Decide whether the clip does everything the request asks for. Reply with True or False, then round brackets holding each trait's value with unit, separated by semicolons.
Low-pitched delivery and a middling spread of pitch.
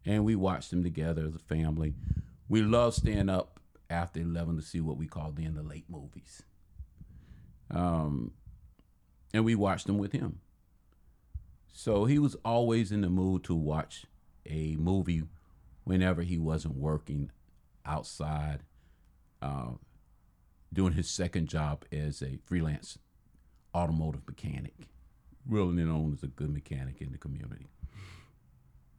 True (80 Hz; 3.5 semitones)